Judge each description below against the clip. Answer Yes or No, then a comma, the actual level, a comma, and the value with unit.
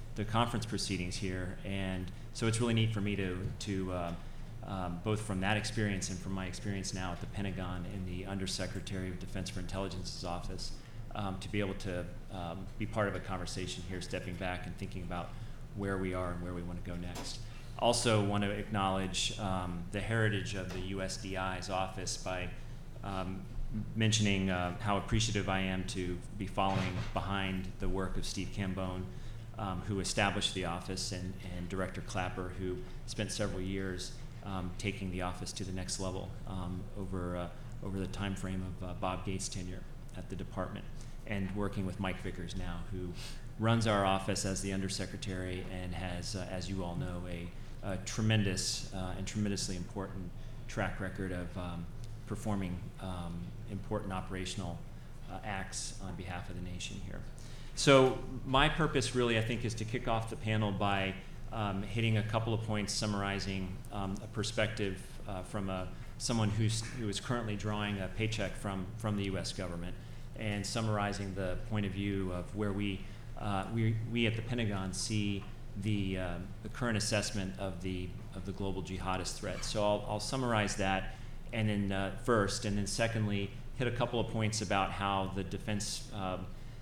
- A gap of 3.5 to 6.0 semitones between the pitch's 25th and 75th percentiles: No, average, 2.9 semitones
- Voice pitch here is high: No, low, 100 Hz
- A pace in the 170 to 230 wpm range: Yes, average, 180 wpm